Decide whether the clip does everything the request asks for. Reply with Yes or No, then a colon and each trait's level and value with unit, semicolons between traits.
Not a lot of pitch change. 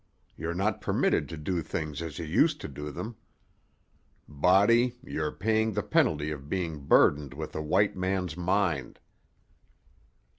No: average, 4.4 semitones